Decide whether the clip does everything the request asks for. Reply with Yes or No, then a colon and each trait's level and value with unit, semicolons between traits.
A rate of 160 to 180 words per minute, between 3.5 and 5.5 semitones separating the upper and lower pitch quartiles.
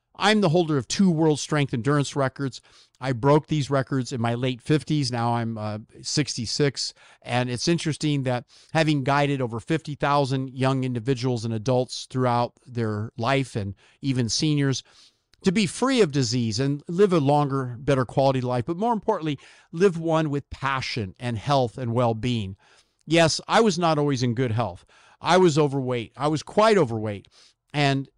Yes: average, 170 wpm; average, 3.8 semitones